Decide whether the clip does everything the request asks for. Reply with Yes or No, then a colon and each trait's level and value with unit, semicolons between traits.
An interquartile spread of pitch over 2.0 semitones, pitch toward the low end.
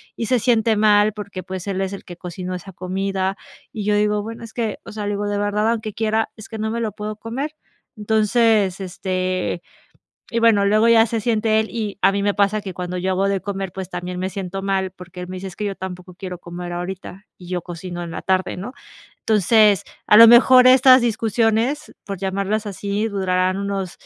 No: average, 2.8 semitones; high, 200 Hz